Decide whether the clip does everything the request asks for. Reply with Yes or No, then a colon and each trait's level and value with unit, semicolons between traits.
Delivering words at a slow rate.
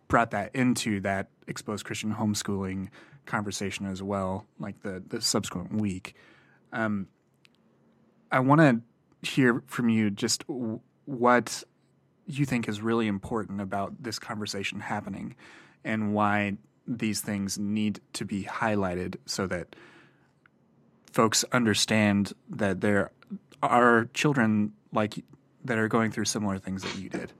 Yes: slow, 130 wpm